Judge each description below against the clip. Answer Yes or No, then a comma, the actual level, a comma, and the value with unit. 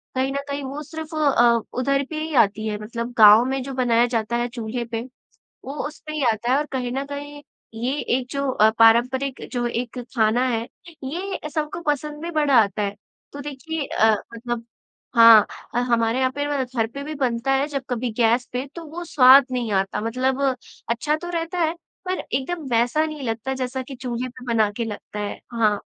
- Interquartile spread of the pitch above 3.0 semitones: Yes, average, 3.7 semitones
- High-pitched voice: Yes, very high, 255 Hz